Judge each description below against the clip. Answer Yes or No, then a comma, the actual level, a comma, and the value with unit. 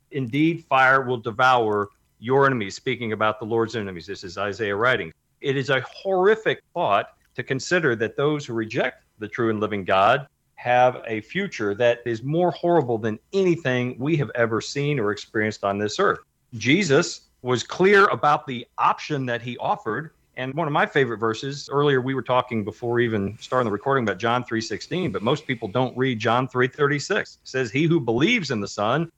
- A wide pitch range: No, average, 4.1 semitones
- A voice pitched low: Yes, low, 125 Hz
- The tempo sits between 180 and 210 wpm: Yes, average, 185 wpm